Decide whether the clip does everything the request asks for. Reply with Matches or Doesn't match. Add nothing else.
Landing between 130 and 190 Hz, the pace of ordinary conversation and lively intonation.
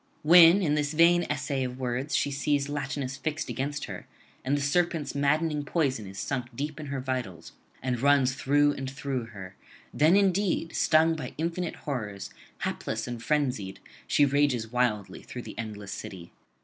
Doesn't match